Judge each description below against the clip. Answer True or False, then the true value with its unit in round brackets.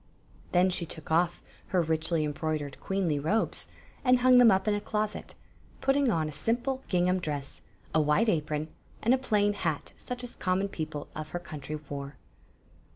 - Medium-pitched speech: True (175 Hz)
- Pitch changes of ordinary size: False (5.7 semitones)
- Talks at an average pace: True (170 wpm)